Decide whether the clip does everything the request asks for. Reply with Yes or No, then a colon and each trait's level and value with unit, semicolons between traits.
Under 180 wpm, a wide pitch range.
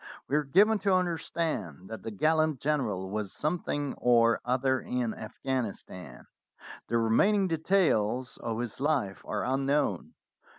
Yes: slow, 135 wpm; wide, 6.0 semitones